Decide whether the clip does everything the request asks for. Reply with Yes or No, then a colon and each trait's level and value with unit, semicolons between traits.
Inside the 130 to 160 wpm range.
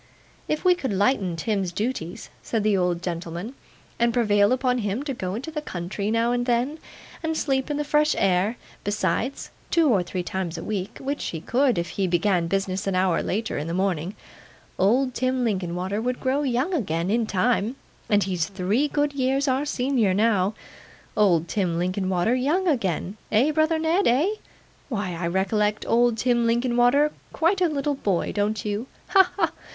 No: average, 180 wpm